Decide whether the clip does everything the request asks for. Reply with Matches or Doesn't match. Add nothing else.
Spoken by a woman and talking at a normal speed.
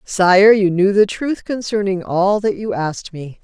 Matches